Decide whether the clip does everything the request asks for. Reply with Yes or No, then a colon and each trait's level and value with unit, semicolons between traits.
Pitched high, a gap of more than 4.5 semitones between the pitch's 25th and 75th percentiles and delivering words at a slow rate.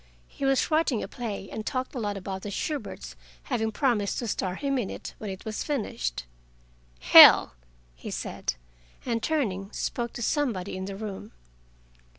No: high, 220 Hz; average, 4.9 semitones; average, 165 wpm